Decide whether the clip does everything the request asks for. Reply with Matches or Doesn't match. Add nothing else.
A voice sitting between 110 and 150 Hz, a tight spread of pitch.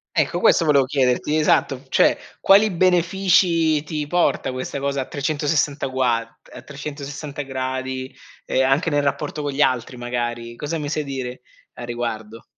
Doesn't match